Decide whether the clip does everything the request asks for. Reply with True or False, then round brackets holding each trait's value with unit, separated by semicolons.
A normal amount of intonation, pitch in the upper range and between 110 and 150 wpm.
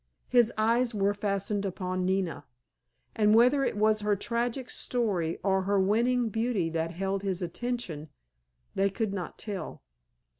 True (3.5 semitones; 205 Hz; 145 wpm)